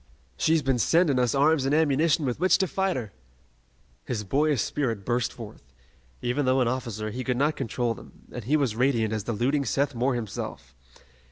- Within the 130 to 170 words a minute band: No, average, 190 wpm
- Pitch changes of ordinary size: Yes, average, 3.7 semitones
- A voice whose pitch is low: Yes, low, 130 Hz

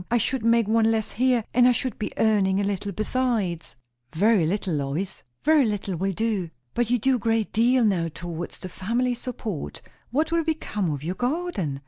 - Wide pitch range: No, average, 4.7 semitones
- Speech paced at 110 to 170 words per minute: No, average, 190 wpm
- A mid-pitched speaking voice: No, high, 220 Hz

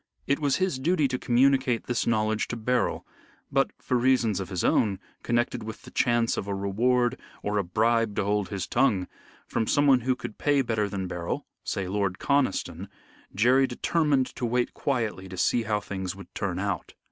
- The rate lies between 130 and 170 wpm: No, average, 185 wpm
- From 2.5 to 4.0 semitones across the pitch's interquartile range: No, average, 4.4 semitones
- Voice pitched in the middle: No, low, 115 Hz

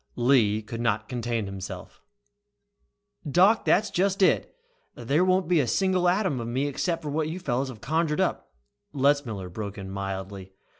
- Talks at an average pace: Yes, average, 160 wpm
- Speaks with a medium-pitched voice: No, low, 130 Hz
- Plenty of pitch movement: Yes, wide, 8.4 semitones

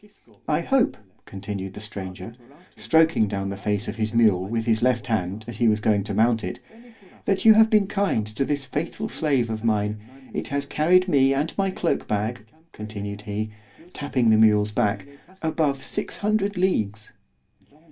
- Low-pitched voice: Yes, low, 115 Hz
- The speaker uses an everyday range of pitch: No, wide, 6.2 semitones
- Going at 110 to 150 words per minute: No, average, 170 wpm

